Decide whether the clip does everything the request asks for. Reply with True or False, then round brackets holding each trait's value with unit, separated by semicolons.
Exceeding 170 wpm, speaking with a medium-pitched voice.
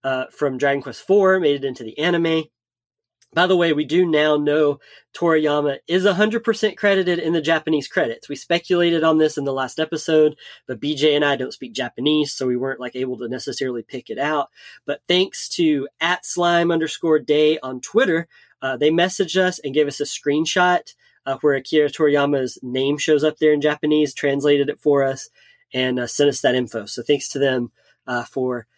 True (195 wpm; 150 Hz)